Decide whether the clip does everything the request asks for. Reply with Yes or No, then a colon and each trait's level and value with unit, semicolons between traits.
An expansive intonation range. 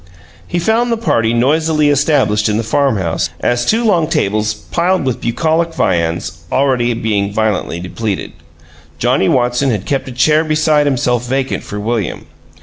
Yes: wide, 6.3 semitones